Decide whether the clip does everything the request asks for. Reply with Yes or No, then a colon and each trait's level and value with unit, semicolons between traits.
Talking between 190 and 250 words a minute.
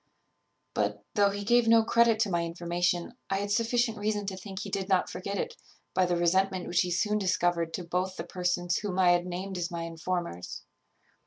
Yes: average, 200 wpm